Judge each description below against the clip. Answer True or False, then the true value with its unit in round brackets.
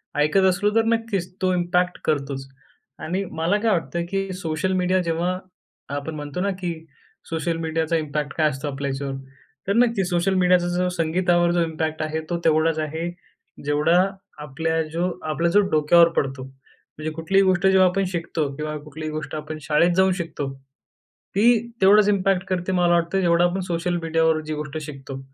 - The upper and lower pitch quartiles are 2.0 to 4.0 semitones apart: True (3.0 semitones)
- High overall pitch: False (170 Hz)